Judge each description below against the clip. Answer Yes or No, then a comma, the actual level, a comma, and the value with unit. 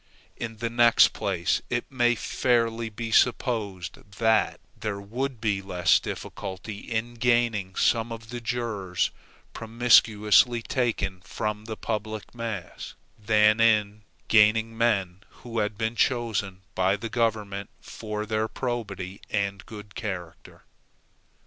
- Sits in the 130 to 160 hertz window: No, low, 110 Hz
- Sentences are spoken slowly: Yes, slow, 125 wpm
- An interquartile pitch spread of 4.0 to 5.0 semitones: No, narrow, 2.6 semitones